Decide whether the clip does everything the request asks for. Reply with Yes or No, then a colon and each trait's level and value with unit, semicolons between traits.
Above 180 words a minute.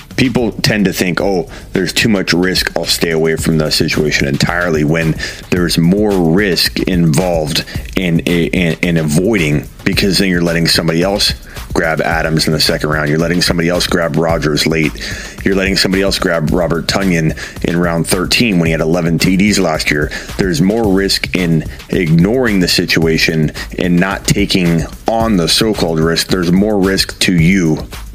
No: average, 170 wpm